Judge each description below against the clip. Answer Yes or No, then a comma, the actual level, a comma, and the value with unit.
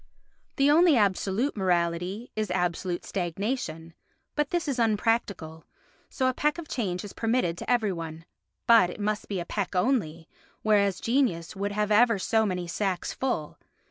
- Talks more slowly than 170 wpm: Yes, average, 160 wpm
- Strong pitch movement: No, average, 5.0 semitones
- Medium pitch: No, high, 205 Hz